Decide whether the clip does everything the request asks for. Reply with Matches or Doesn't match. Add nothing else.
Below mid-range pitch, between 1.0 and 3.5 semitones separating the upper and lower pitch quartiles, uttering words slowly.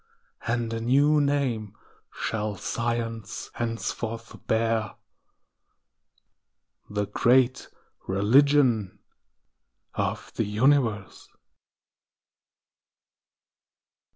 Matches